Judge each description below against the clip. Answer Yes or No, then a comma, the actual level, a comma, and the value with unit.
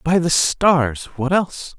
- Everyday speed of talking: Yes, average, 170 wpm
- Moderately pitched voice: Yes, medium, 155 Hz